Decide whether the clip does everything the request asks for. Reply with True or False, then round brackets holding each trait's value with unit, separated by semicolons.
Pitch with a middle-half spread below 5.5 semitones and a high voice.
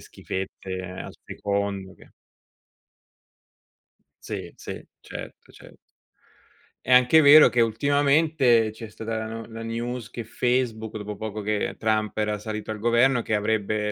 False (2.4 semitones; 110 Hz)